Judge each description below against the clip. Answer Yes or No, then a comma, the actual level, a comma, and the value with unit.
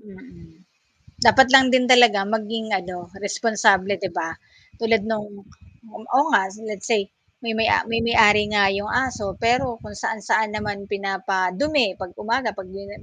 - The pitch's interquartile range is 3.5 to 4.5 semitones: No, narrow, 2.6 semitones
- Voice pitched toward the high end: Yes, high, 210 Hz